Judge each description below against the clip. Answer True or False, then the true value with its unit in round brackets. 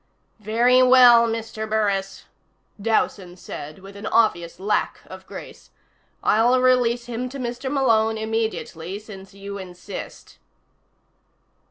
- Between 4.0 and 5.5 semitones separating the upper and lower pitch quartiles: False (3.4 semitones)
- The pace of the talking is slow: True (115 wpm)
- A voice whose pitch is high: True (220 Hz)